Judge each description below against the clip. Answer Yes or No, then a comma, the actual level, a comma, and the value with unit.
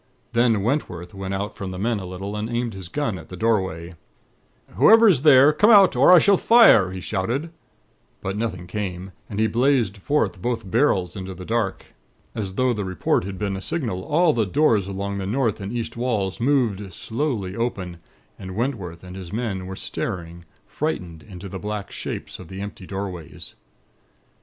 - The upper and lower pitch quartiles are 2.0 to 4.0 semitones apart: No, average, 4.5 semitones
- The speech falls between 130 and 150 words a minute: No, average, 185 wpm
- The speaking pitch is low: Yes, low, 100 Hz